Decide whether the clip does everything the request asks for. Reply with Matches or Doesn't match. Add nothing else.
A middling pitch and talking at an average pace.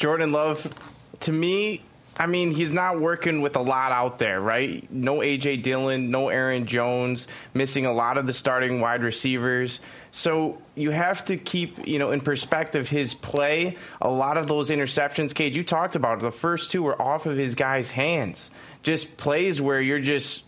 Matches